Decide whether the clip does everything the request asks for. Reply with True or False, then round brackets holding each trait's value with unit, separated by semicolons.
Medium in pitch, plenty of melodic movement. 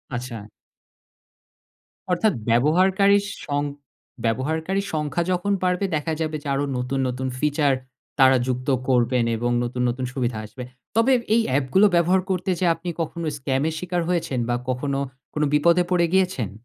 True (150 Hz; 5.8 semitones)